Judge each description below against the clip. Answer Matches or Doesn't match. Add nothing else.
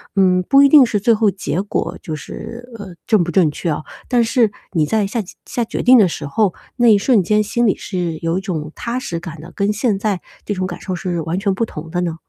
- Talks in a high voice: Matches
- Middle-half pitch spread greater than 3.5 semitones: Matches